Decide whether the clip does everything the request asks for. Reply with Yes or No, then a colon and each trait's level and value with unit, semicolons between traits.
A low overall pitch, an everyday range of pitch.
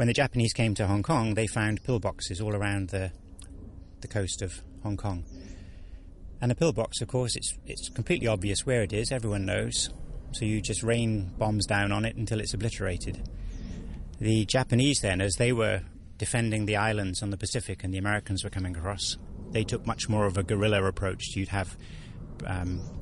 Yes: low, 105 Hz; average, 3.0 semitones